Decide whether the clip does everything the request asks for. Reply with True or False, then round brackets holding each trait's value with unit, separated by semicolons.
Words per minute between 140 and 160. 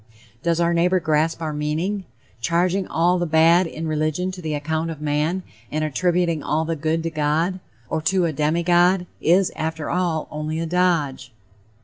False (180 wpm)